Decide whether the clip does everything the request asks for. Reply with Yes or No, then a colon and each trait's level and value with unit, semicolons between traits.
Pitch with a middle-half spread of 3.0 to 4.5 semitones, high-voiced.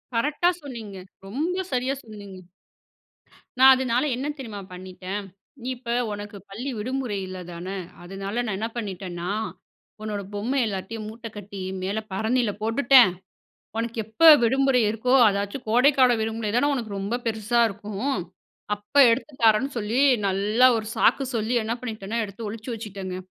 Yes: average, 3.7 semitones; high, 220 Hz